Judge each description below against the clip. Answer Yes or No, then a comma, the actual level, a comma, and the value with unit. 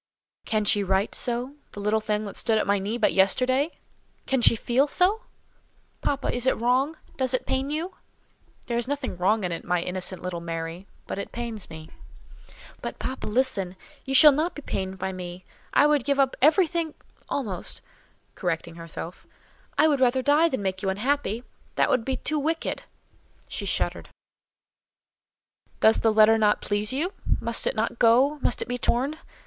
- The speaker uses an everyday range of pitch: No, wide, 6.2 semitones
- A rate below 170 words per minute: No, average, 175 wpm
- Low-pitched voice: No, high, 235 Hz